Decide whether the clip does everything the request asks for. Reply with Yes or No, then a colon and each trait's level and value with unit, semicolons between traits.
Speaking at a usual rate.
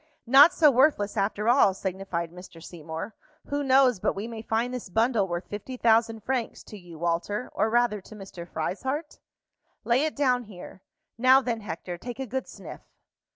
Yes: average, 175 wpm